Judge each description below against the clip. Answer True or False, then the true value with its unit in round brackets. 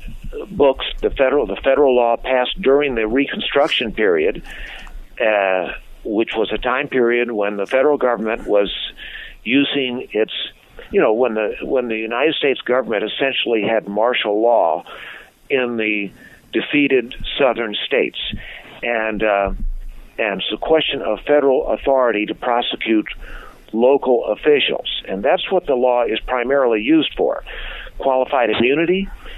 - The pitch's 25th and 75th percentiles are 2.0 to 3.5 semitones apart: False (4.7 semitones)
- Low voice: True (125 Hz)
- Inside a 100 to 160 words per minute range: True (135 wpm)